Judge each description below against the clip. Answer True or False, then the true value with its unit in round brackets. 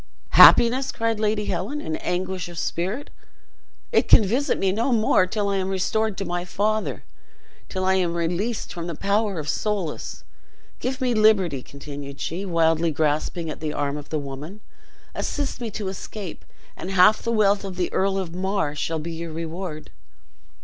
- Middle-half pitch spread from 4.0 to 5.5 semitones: True (4.4 semitones)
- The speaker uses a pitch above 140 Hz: True (185 Hz)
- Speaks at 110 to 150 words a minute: False (170 wpm)